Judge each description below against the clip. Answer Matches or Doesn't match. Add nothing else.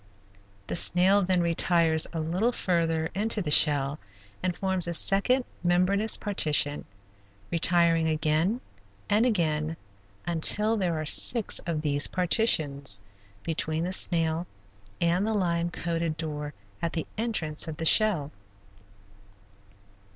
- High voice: Doesn't match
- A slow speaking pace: Matches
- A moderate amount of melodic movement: Matches